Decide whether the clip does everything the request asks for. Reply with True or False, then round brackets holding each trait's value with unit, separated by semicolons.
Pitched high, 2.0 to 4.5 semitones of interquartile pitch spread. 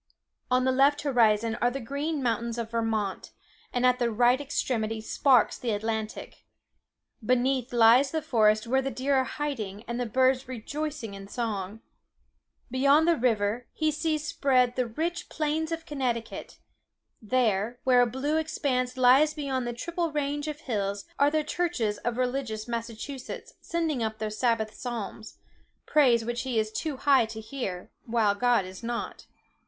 True (245 Hz; 3.9 semitones)